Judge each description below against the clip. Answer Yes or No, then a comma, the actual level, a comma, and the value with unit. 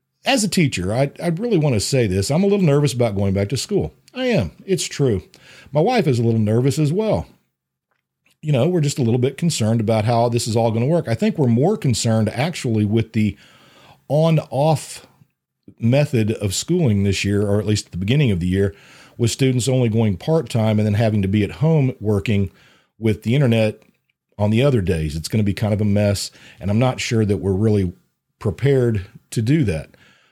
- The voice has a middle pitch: No, low, 120 Hz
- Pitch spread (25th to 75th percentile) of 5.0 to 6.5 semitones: Yes, wide, 5.6 semitones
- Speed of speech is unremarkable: No, fast, 215 wpm